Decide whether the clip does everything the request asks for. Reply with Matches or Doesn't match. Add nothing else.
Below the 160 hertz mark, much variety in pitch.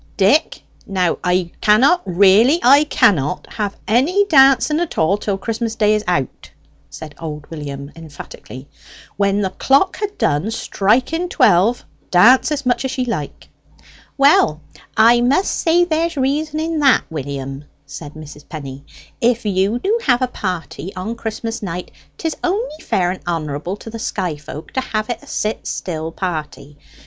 Doesn't match